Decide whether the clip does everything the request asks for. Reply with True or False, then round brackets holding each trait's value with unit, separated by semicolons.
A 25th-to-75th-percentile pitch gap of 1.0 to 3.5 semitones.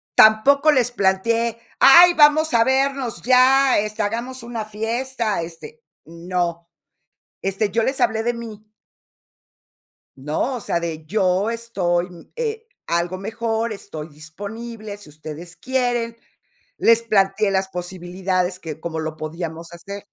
False (5.1 semitones)